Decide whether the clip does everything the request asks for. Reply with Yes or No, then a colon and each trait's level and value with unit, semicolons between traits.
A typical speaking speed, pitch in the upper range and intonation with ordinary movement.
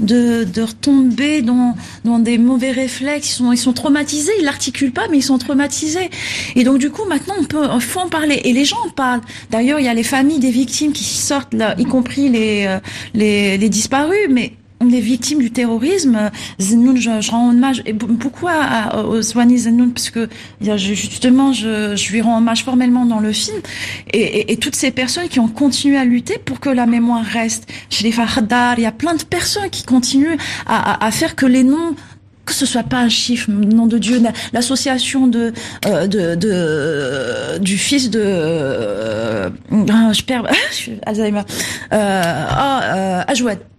Yes: average, 190 wpm; high, 245 Hz; average, 3.6 semitones